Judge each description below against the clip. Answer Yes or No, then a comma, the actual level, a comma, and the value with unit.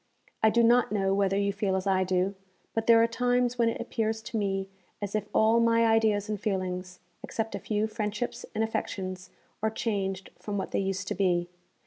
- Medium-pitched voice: No, high, 210 Hz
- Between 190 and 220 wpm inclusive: Yes, average, 200 wpm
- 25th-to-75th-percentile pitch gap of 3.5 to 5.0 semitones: No, average, 2.7 semitones